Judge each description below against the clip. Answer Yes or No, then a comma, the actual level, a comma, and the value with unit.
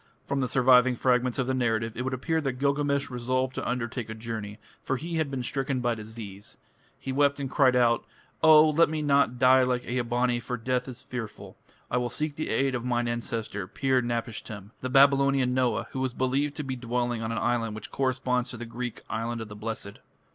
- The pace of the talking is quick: Yes, fast, 210 wpm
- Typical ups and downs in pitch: No, narrow, 2.3 semitones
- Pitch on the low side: Yes, low, 125 Hz